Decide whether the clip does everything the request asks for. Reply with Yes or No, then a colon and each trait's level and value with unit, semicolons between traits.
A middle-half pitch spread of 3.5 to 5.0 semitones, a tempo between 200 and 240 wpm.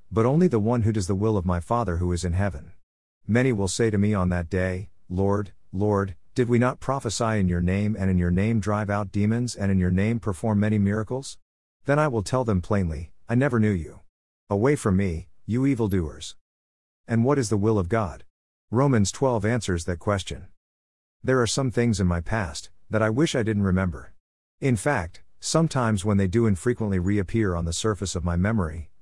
Yes: average, 4.1 semitones; fast, 205 wpm